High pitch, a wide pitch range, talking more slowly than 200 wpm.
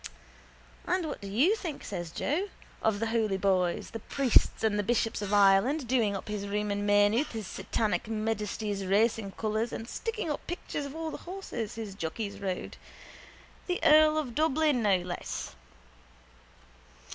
Yes: high, 220 Hz; wide, 5.8 semitones; average, 160 wpm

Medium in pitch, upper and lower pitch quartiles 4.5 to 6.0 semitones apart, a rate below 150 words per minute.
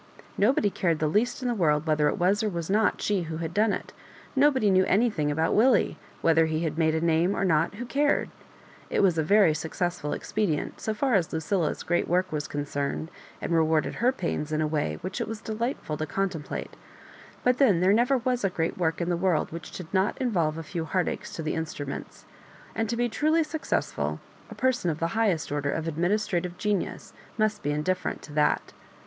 No: medium, 175 Hz; average, 5.2 semitones; fast, 205 wpm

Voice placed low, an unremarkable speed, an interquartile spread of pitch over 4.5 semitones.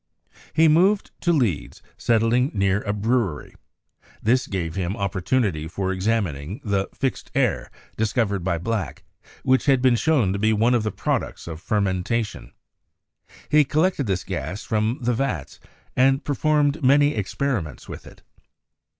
Yes: low, 110 Hz; average, 150 wpm; wide, 5.5 semitones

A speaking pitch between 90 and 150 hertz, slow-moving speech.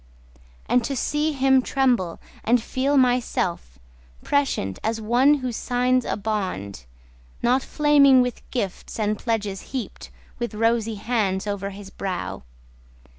No: high, 235 Hz; slow, 125 wpm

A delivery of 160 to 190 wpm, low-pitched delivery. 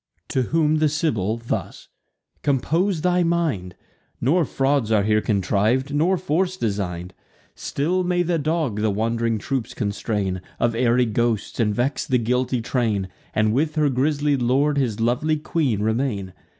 No: average, 150 wpm; low, 125 Hz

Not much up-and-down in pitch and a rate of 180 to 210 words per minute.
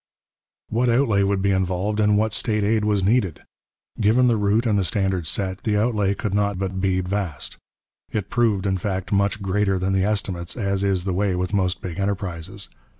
Yes: narrow, 1.9 semitones; average, 195 wpm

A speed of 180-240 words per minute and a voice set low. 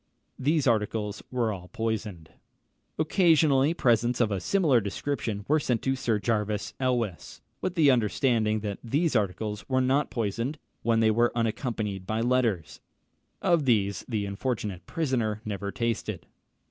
No: average, 140 wpm; low, 115 Hz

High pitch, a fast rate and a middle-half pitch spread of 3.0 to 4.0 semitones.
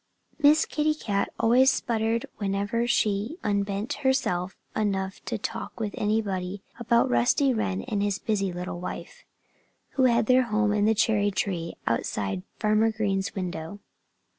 No: high, 210 Hz; average, 140 wpm; average, 3.3 semitones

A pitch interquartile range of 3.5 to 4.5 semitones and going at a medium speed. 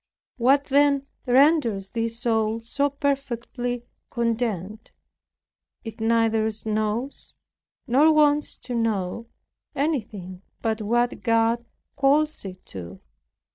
No: average, 4.0 semitones; slow, 95 wpm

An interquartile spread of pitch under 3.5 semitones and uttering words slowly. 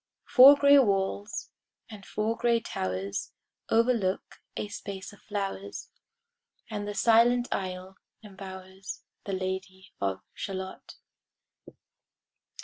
Yes: average, 3.0 semitones; slow, 100 wpm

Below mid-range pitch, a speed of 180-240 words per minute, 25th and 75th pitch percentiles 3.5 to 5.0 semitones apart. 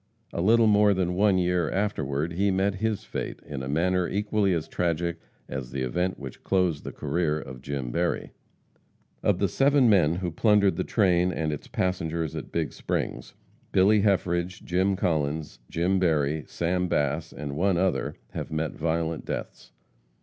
No: very low, 90 Hz; average, 165 wpm; average, 3.8 semitones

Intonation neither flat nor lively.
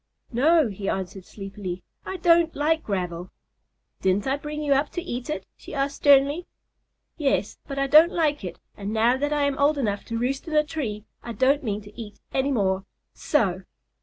No: wide, 6.5 semitones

